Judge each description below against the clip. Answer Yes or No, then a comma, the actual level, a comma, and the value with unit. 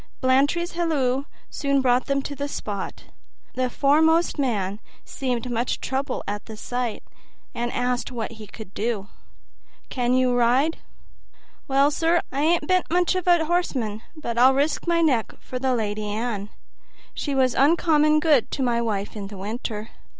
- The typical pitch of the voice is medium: No, very high, 255 Hz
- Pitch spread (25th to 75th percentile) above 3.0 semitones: Yes, average, 4.5 semitones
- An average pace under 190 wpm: Yes, average, 155 wpm